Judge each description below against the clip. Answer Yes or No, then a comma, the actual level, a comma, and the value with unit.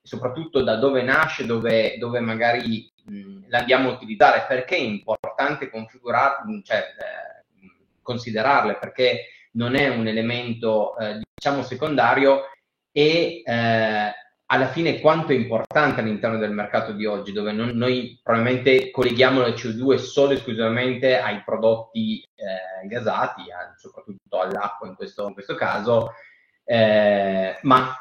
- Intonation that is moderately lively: Yes, average, 3.7 semitones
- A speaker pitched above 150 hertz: No, low, 125 Hz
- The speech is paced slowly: No, average, 130 wpm